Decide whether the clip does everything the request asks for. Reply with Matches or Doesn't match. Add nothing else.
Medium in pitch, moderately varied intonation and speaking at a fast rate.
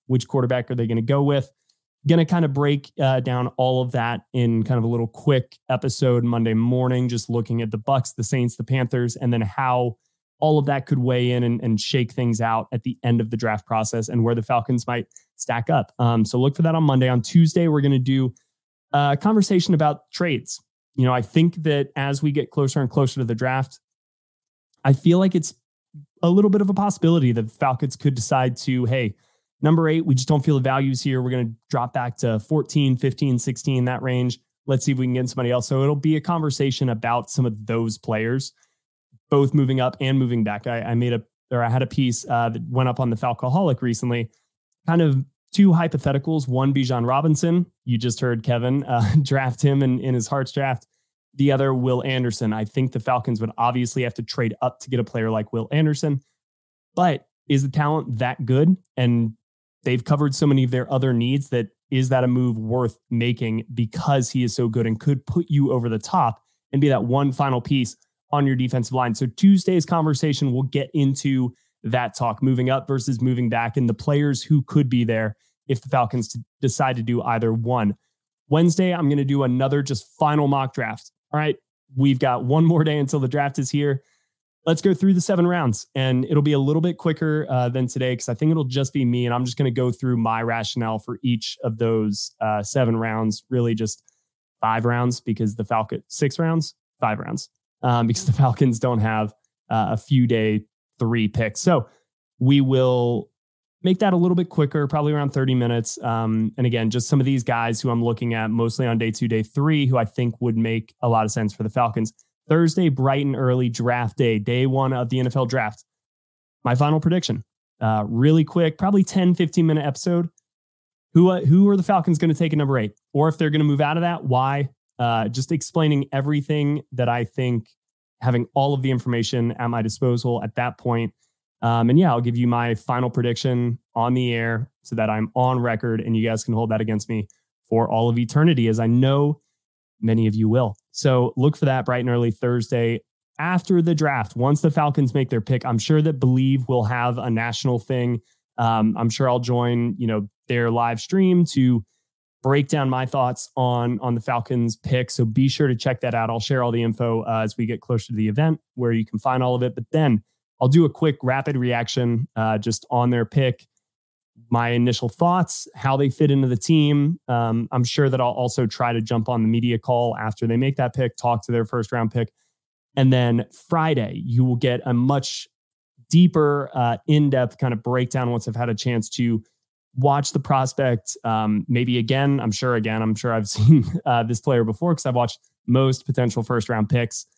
Doesn't match